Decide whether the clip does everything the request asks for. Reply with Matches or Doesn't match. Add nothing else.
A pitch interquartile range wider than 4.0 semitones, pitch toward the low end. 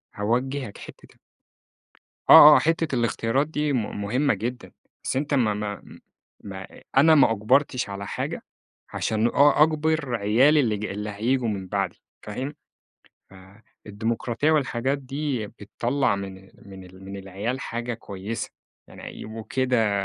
Matches